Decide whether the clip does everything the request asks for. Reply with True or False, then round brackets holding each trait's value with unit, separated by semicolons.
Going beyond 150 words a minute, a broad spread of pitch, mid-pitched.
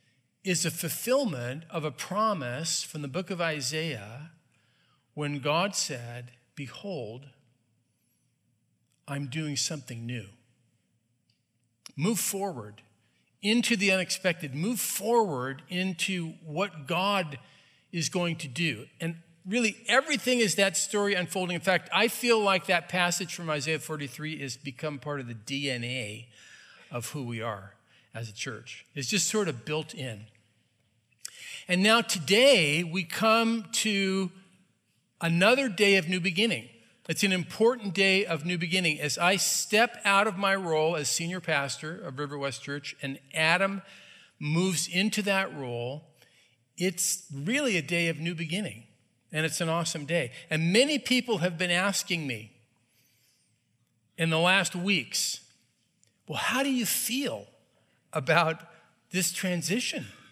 False (135 wpm; 6.6 semitones; 165 Hz)